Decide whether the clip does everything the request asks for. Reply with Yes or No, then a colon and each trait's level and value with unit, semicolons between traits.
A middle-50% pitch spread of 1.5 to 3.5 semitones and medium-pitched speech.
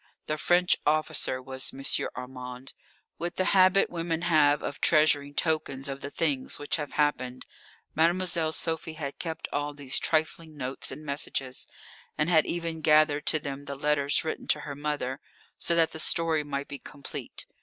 Yes: narrow, 2.5 semitones; medium, 150 Hz